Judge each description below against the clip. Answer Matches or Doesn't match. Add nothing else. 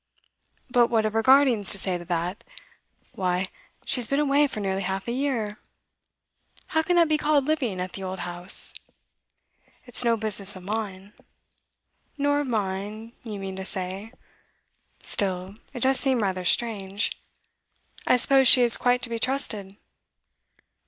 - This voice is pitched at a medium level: Doesn't match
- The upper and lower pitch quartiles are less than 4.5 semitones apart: Doesn't match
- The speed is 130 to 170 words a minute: Matches